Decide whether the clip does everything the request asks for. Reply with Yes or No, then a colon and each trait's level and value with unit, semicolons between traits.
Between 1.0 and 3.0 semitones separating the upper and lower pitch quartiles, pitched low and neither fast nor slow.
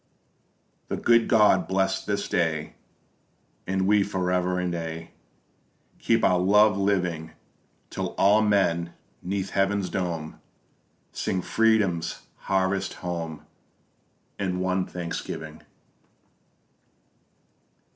No: average, 2.7 semitones; very low, 95 Hz; slow, 95 wpm